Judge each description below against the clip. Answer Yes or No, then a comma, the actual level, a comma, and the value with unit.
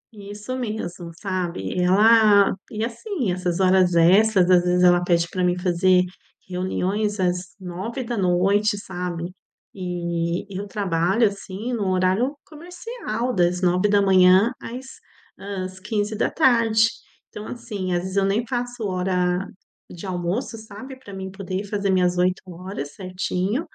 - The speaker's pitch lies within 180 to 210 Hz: Yes, high, 190 Hz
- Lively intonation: No, average, 3.2 semitones